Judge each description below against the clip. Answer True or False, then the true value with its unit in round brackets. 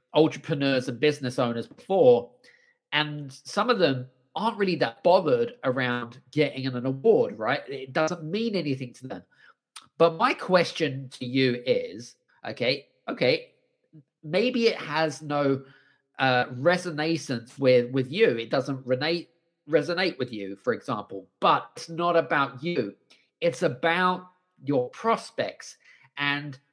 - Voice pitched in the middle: True (150 Hz)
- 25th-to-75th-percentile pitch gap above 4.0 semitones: True (5.2 semitones)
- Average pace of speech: False (130 wpm)